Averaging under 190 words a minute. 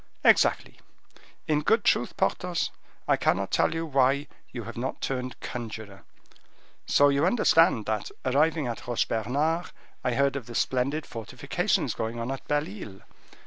Yes: average, 150 wpm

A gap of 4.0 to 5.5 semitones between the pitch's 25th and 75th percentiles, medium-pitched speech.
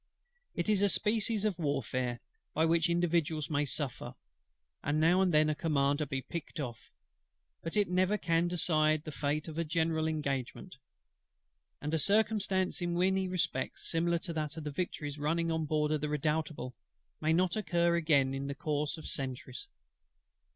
No: average, 2.9 semitones; medium, 160 Hz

